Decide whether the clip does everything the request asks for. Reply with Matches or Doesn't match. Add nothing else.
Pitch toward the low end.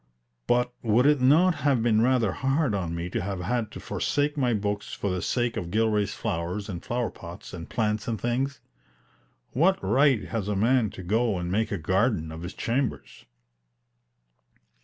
Matches